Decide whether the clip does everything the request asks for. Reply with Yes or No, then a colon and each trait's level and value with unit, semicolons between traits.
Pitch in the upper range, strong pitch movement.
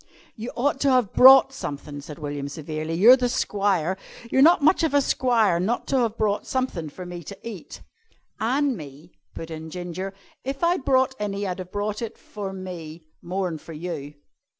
Yes: high, 195 Hz; wide, 7.4 semitones